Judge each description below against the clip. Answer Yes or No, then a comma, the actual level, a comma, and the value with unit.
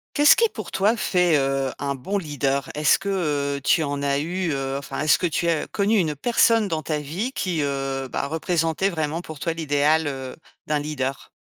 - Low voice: No, medium, 155 Hz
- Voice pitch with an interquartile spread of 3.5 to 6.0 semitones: Yes, average, 4.1 semitones